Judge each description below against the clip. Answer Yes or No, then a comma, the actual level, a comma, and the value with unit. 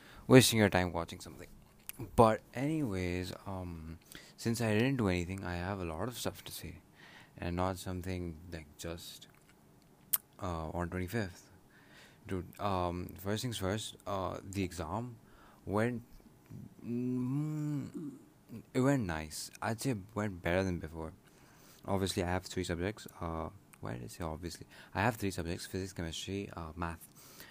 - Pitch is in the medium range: No, very low, 95 Hz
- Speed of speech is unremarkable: Yes, average, 150 wpm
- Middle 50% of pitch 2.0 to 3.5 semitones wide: No, average, 3.9 semitones